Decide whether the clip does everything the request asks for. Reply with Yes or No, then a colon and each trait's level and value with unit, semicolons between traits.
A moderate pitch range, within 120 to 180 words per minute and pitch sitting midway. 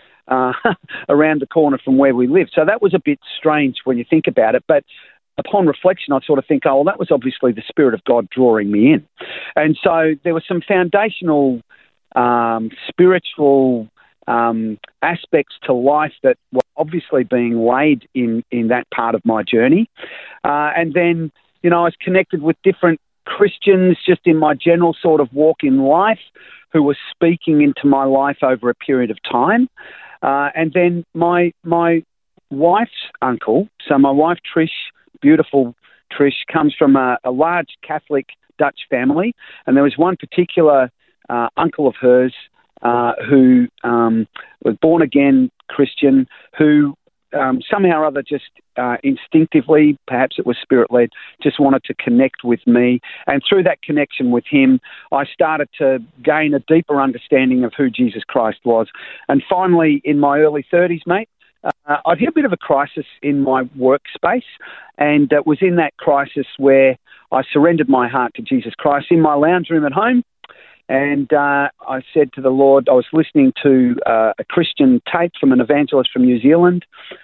Yes: average, 4.5 semitones; average, 175 wpm; medium, 145 Hz